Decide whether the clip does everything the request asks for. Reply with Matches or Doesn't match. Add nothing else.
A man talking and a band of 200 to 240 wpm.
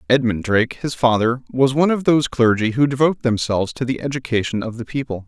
Matches